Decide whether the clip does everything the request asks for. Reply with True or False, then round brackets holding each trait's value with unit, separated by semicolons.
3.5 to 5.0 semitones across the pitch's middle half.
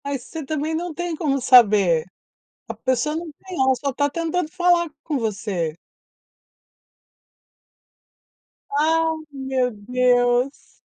True (4.7 semitones)